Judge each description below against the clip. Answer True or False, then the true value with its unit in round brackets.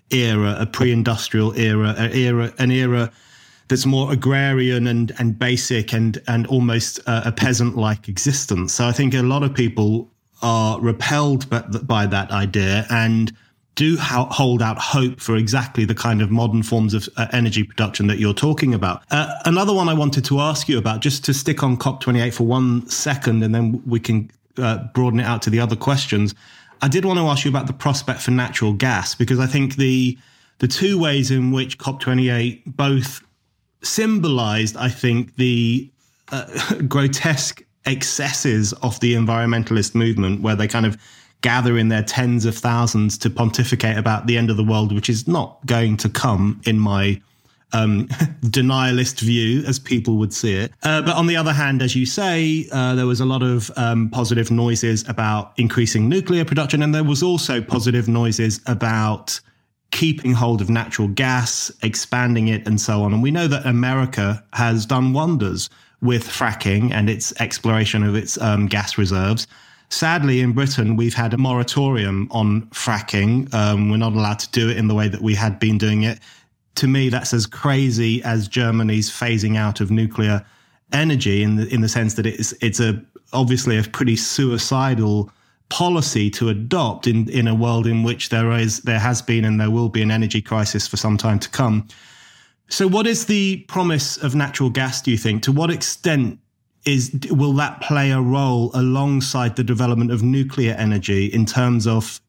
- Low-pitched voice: True (120 Hz)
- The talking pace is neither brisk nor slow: True (185 wpm)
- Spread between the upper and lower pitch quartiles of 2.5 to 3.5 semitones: True (3.0 semitones)